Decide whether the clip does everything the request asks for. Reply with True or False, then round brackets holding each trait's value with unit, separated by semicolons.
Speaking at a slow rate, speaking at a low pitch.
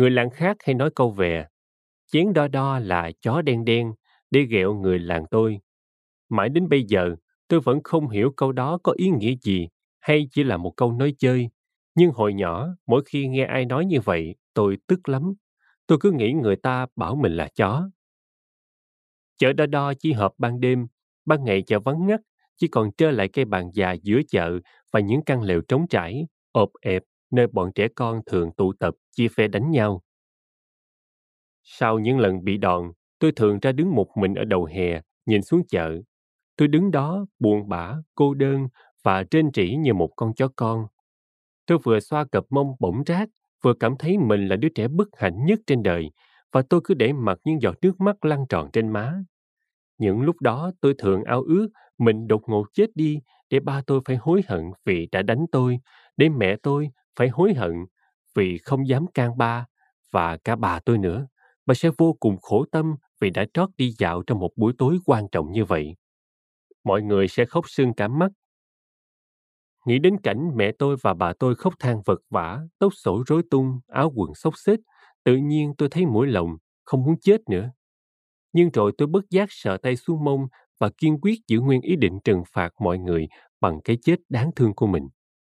False (200 wpm; 125 Hz)